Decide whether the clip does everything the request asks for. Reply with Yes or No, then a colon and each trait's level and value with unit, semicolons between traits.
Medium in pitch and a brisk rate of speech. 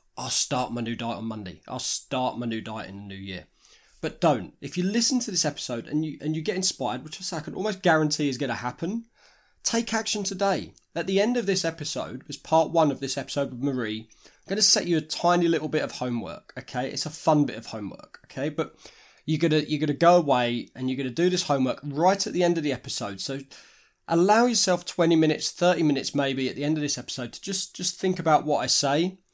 Yes: medium, 155 Hz; fast, 235 wpm